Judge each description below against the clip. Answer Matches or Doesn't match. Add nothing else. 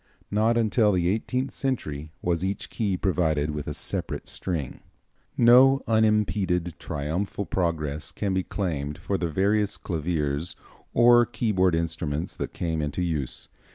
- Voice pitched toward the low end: Matches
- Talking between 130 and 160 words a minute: Matches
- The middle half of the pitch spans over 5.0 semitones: Matches